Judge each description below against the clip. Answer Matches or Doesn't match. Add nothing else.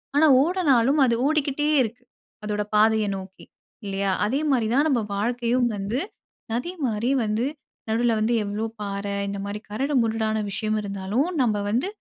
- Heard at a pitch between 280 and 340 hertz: Doesn't match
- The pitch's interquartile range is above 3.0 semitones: Matches